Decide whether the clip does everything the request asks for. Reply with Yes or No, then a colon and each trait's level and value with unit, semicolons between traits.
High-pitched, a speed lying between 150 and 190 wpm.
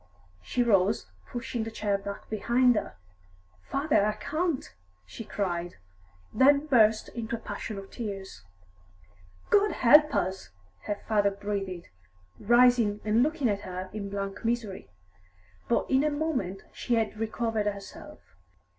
No: high, 215 Hz; slow, 135 wpm